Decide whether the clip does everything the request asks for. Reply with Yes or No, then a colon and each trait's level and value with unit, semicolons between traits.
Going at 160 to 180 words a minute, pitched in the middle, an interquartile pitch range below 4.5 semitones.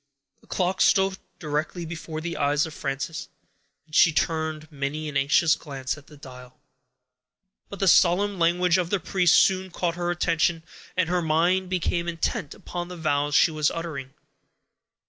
Yes: average, 165 wpm; medium, 165 Hz; average, 2.9 semitones